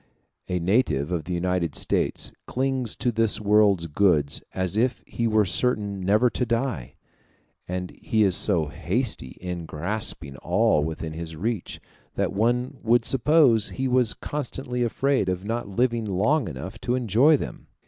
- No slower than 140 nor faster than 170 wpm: Yes, average, 160 wpm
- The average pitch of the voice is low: Yes, low, 105 Hz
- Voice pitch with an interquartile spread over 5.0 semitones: Yes, wide, 5.4 semitones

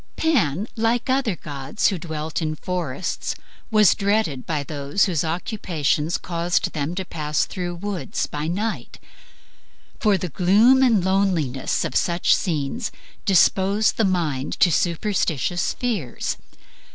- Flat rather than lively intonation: No, average, 5.0 semitones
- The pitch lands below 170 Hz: No, medium, 180 Hz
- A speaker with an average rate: No, slow, 130 wpm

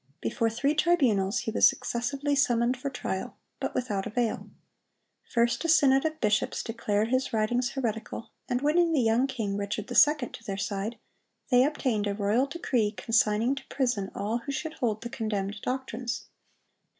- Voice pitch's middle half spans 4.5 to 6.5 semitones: No, average, 4.0 semitones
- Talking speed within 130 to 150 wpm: No, average, 160 wpm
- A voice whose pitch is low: No, high, 235 Hz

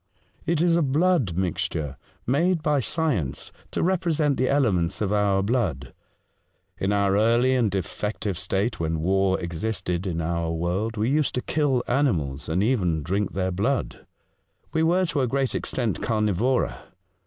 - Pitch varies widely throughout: Yes, wide, 7.1 semitones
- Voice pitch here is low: Yes, low, 105 Hz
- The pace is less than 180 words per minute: Yes, average, 155 wpm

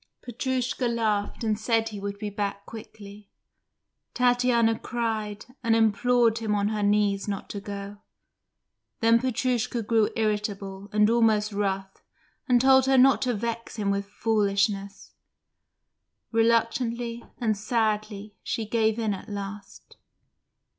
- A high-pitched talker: Yes, high, 215 Hz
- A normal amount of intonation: No, narrow, 2.3 semitones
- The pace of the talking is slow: Yes, slow, 125 wpm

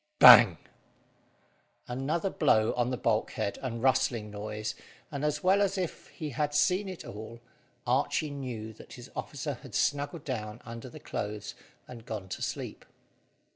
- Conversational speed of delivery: Yes, average, 150 wpm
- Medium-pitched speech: No, low, 125 Hz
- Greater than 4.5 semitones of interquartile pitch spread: Yes, wide, 5.4 semitones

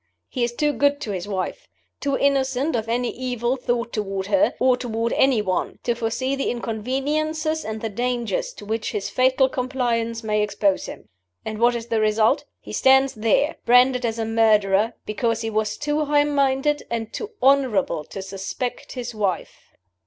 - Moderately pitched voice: No, high, 240 Hz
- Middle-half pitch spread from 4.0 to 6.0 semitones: No, average, 3.5 semitones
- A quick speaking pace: No, average, 175 wpm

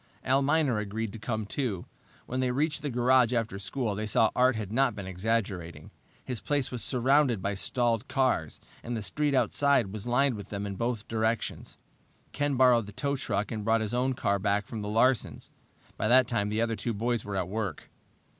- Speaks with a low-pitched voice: Yes, low, 115 Hz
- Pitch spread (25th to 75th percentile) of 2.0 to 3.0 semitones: No, average, 3.9 semitones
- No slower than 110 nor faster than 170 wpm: No, average, 200 wpm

